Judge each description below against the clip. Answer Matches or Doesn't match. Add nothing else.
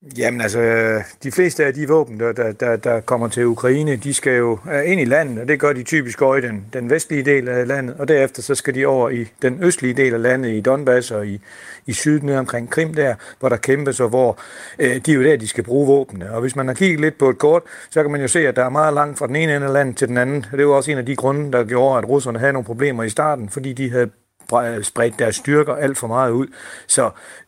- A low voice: Matches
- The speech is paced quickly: Matches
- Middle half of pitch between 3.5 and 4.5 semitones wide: Doesn't match